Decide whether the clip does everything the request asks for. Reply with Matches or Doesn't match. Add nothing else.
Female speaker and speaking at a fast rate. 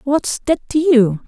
Doesn't match